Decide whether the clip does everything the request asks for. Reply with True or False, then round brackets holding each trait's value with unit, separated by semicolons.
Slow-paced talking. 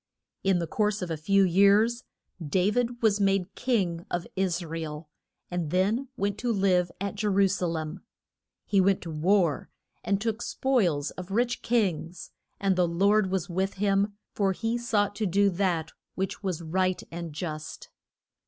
False (170 wpm)